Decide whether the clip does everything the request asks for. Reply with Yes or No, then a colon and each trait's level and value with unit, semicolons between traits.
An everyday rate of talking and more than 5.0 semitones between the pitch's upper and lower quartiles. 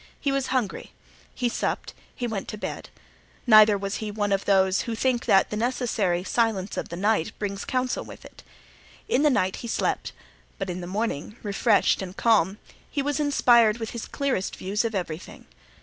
No: average, 185 wpm; average, 3.8 semitones